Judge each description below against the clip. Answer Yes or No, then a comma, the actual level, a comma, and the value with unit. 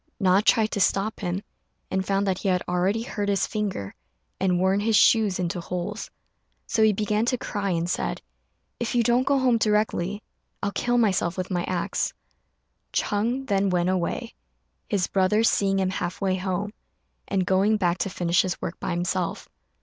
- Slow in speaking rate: No, average, 180 wpm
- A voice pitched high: Yes, high, 195 Hz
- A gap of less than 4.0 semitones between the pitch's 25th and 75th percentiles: Yes, average, 2.7 semitones